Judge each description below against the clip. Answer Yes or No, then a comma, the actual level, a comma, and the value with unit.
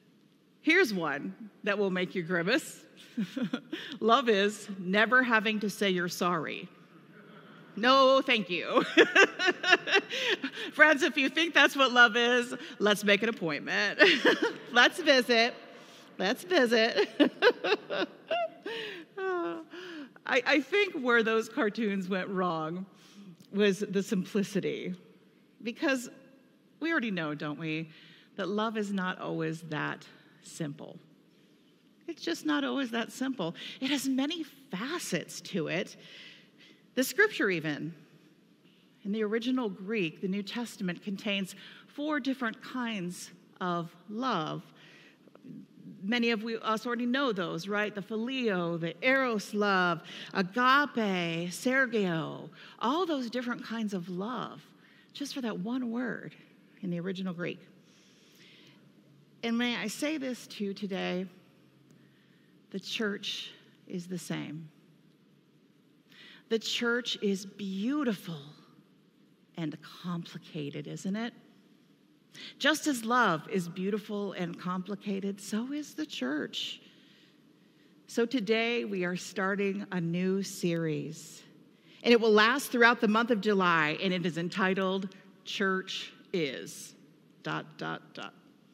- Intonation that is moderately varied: No, wide, 5.7 semitones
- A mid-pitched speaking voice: No, high, 215 Hz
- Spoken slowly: Yes, slow, 120 wpm